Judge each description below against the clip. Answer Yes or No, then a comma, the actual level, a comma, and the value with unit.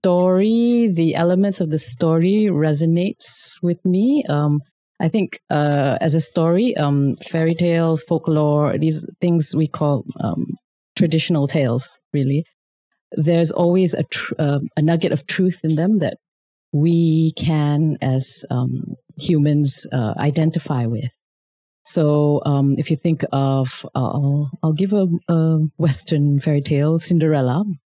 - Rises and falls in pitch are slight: No, average, 3.1 semitones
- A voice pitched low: No, medium, 160 Hz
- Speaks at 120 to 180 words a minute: Yes, slow, 135 wpm